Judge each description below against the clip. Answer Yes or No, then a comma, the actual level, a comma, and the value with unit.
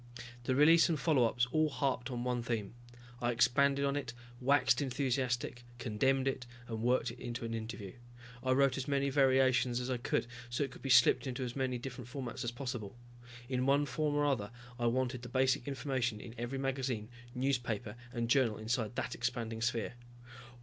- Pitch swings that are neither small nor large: No, narrow, 2.2 semitones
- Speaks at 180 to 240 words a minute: Yes, average, 185 wpm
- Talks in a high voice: No, low, 125 Hz